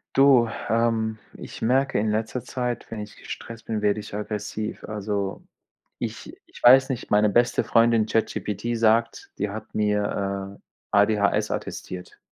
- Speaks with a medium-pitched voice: No, low, 110 Hz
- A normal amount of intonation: No, narrow, 2.0 semitones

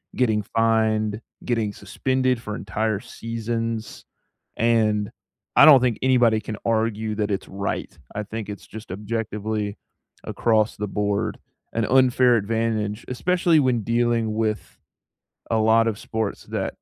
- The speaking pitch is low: Yes, low, 110 Hz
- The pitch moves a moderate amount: No, narrow, 1.7 semitones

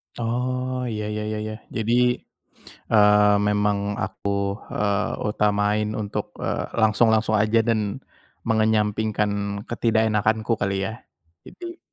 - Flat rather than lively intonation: Yes, narrow, 1.5 semitones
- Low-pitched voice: Yes, low, 110 Hz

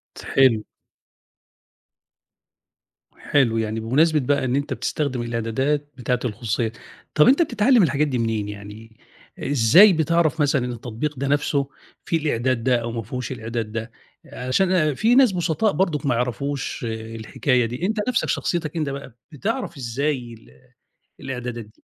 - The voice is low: Yes, low, 130 Hz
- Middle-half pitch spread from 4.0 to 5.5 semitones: Yes, average, 4.7 semitones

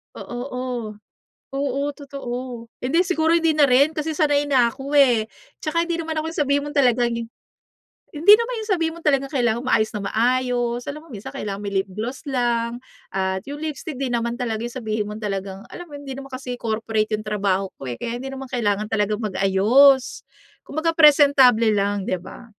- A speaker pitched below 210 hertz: No, very high, 250 Hz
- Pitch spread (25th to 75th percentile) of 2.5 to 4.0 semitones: No, average, 4.8 semitones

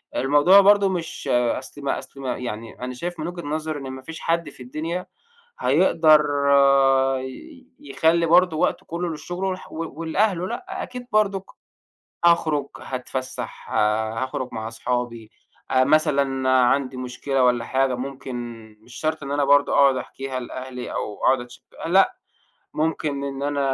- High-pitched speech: No, medium, 140 Hz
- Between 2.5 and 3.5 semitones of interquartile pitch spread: No, average, 4.6 semitones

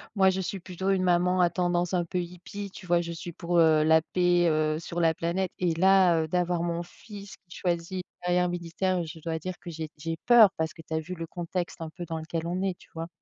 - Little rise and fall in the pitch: Yes, narrow, 1.8 semitones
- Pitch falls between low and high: Yes, medium, 175 Hz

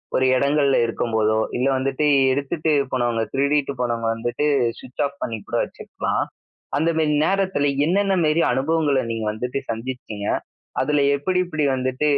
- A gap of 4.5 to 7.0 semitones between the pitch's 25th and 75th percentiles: No, average, 3.8 semitones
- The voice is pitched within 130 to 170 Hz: Yes, low, 135 Hz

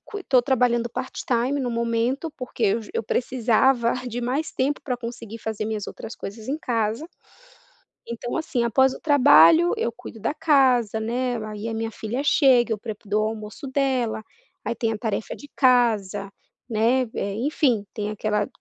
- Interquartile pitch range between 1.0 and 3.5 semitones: Yes, average, 3.0 semitones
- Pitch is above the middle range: Yes, high, 235 Hz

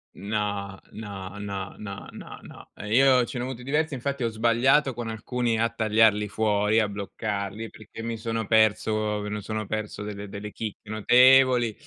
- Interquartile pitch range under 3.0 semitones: Yes, narrow, 2.4 semitones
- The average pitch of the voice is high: No, low, 110 Hz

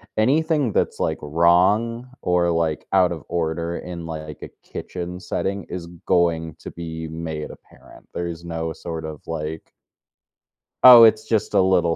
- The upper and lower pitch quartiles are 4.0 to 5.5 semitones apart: No, average, 2.7 semitones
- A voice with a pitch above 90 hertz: No, very low, 85 Hz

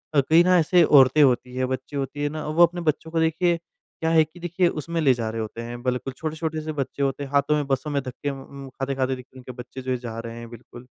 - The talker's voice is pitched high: No, medium, 140 Hz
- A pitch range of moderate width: Yes, average, 3.8 semitones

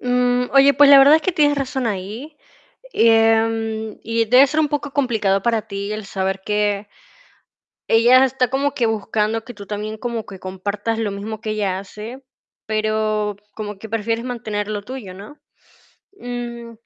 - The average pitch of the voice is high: Yes, high, 225 Hz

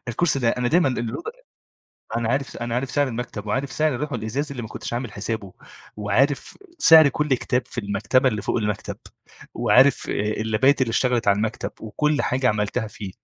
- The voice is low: Yes, low, 120 Hz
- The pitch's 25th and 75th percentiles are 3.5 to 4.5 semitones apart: Yes, average, 3.8 semitones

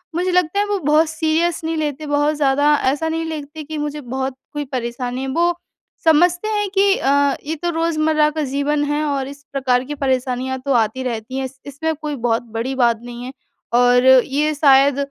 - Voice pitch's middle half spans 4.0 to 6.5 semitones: No, average, 3.3 semitones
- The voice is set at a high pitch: Yes, very high, 290 Hz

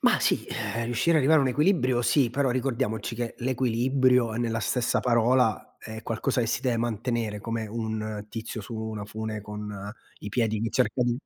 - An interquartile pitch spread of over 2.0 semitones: Yes, narrow, 2.4 semitones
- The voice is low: Yes, low, 115 Hz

